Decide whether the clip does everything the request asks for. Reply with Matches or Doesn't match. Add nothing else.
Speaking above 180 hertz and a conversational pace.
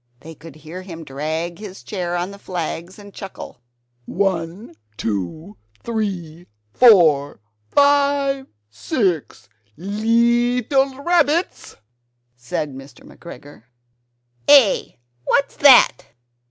Doesn't match